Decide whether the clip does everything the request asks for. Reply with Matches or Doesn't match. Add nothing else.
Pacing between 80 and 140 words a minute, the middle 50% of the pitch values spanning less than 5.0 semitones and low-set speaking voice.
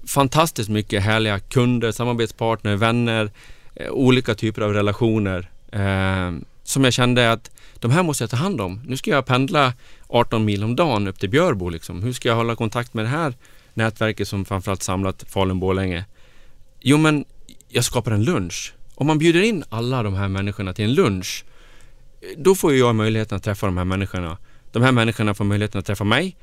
Doesn't match